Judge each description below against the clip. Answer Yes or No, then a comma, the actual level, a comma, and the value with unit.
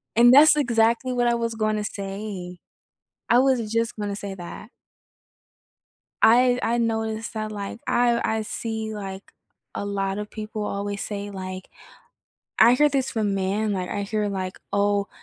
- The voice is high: Yes, high, 215 Hz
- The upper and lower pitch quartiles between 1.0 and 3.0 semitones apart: Yes, narrow, 2.5 semitones